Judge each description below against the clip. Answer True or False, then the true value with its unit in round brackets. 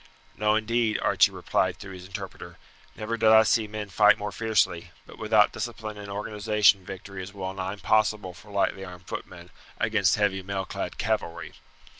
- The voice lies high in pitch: False (105 Hz)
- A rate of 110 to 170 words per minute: True (165 wpm)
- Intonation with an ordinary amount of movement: False (2.2 semitones)